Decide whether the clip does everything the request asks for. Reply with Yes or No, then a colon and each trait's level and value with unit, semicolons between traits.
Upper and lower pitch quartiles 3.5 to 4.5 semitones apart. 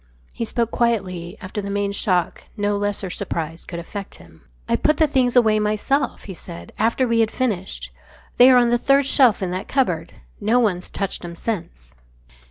No: average, 4.9 semitones